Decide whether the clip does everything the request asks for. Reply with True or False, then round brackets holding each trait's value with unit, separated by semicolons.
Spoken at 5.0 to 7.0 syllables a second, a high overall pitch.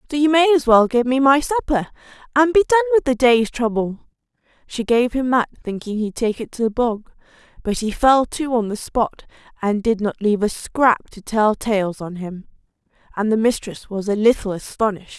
True (5.1 syllables/s; 240 Hz)